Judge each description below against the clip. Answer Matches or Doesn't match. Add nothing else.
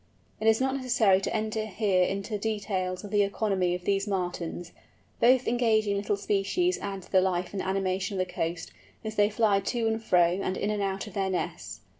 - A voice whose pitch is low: Doesn't match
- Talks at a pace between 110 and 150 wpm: Doesn't match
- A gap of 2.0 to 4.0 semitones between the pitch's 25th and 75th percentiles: Matches